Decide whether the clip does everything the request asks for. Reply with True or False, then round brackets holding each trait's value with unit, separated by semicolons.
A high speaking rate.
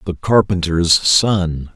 False (105 wpm)